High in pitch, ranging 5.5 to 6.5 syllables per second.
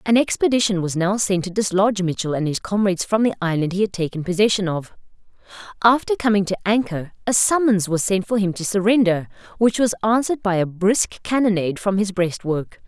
Yes: high, 200 Hz; 5.8 syllables/s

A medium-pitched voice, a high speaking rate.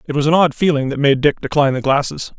Yes: medium, 145 Hz; fast, 275 wpm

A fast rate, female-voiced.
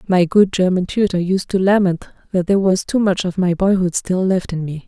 Yes: fast, 235 wpm; female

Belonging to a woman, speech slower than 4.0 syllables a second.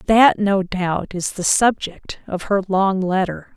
Yes: female; 3.6 syllables/s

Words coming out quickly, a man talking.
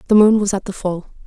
No: fast, 285 wpm; female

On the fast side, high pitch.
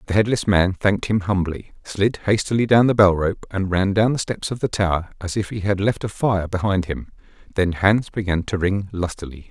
No: fast, 220 wpm; low, 100 Hz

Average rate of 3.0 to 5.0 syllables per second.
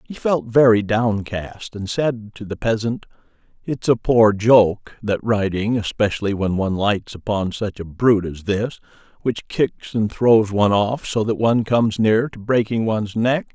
Yes: 4.5 syllables/s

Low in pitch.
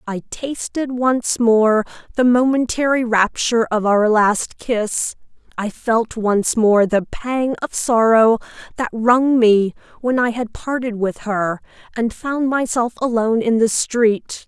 No: high, 230 Hz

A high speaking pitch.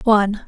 Yes: high, 210 Hz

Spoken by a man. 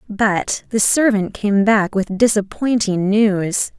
No: female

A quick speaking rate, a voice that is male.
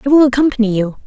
No: fast, 225 wpm; female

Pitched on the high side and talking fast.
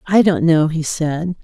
No: medium, 165 Hz; fast, 210 wpm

